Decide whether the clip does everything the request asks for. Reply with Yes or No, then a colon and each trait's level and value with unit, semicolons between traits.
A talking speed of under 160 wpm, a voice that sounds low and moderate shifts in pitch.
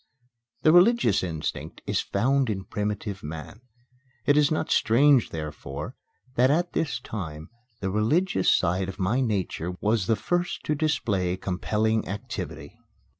No: slow, 135 wpm; low, 105 Hz; wide, 7.0 semitones